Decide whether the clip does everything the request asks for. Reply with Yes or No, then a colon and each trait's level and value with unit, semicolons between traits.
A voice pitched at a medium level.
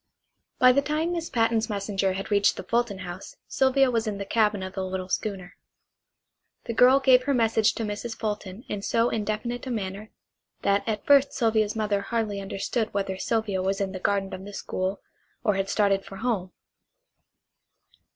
No: high, 210 Hz